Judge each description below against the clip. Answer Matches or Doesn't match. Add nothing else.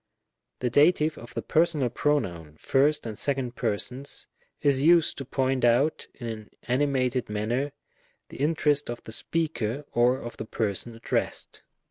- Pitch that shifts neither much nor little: Matches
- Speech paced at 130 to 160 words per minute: Matches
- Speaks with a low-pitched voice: Matches